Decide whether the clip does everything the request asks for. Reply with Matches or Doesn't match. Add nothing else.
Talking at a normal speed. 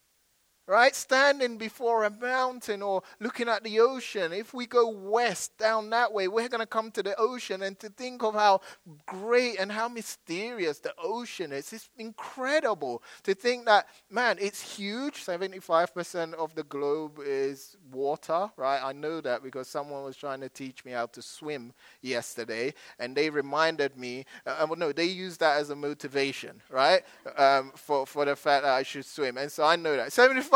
Matches